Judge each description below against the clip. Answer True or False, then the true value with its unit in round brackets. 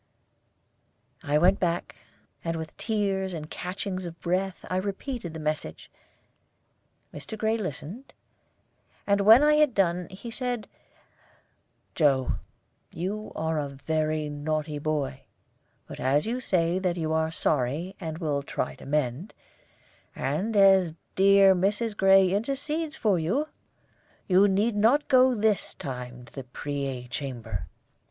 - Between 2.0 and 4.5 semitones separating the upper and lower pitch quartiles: False (5.2 semitones)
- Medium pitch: True (180 Hz)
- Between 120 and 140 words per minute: True (135 wpm)